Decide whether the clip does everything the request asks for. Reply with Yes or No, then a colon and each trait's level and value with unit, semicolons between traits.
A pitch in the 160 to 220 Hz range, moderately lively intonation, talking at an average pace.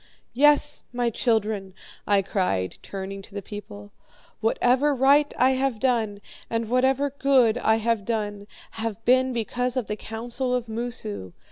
No: high, 230 Hz; average, 3.7 semitones; average, 145 wpm